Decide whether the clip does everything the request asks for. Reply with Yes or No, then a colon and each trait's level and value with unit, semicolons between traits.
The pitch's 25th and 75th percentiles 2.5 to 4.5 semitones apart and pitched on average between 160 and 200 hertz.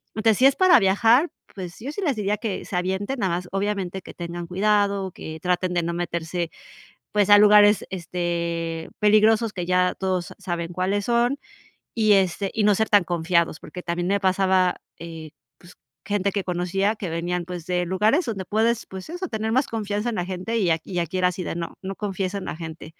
Yes: average, 3.1 semitones; high, 190 Hz